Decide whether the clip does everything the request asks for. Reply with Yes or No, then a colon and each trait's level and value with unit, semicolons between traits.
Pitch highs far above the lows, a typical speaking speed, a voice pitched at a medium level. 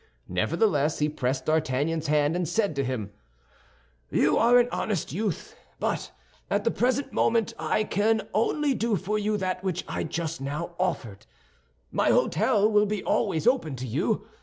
Yes: wide, 6.4 semitones; average, 160 wpm; medium, 180 Hz